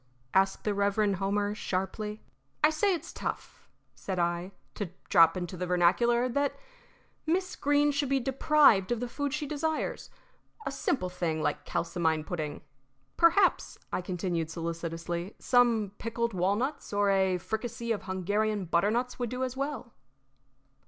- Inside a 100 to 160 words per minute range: Yes, average, 145 wpm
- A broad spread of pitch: Yes, wide, 6.0 semitones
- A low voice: No, high, 205 Hz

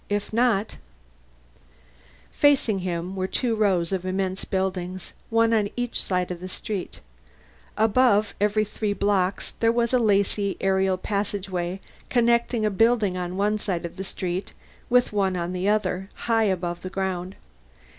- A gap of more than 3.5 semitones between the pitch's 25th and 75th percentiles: No, average, 2.8 semitones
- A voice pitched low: No, high, 195 Hz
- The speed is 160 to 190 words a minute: No, average, 150 wpm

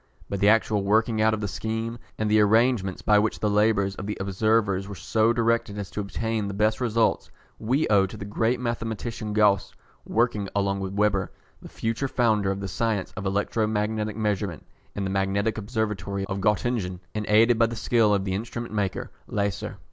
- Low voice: Yes, low, 105 Hz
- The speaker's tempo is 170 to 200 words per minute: Yes, average, 195 wpm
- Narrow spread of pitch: Yes, narrow, 2.2 semitones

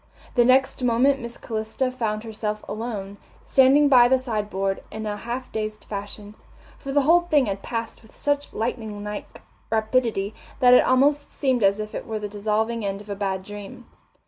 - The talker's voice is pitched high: Yes, high, 225 Hz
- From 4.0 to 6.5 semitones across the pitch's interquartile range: No, average, 3.6 semitones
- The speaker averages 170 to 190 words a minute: Yes, average, 180 wpm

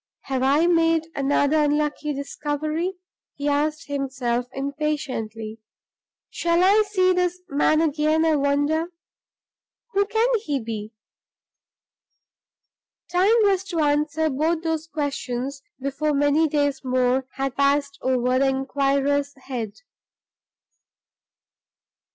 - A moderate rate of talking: No, slow, 105 wpm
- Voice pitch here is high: Yes, very high, 290 Hz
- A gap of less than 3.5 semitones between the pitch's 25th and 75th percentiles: Yes, average, 2.7 semitones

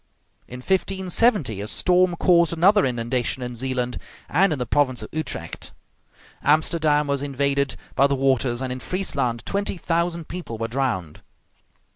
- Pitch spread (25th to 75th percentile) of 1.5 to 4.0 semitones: No, wide, 5.4 semitones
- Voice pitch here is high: No, medium, 140 Hz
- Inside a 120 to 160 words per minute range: Yes, average, 145 wpm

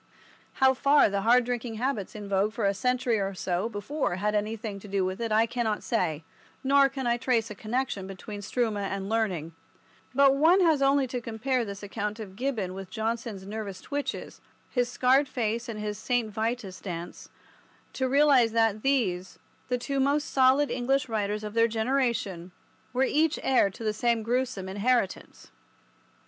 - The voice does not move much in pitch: No, average, 4.1 semitones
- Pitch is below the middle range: No, high, 225 Hz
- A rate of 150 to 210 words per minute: Yes, average, 175 wpm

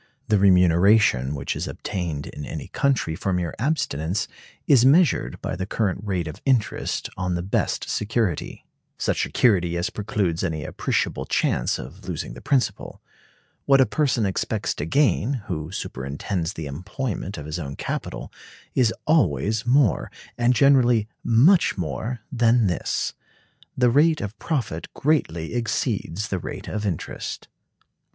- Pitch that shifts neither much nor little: No, wide, 6.4 semitones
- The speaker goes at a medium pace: Yes, average, 145 wpm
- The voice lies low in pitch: Yes, low, 100 Hz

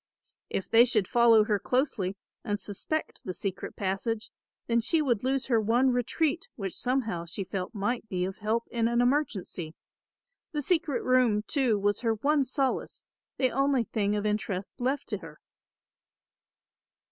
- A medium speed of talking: Yes, average, 160 wpm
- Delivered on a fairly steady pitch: No, average, 4.2 semitones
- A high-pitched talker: Yes, high, 230 Hz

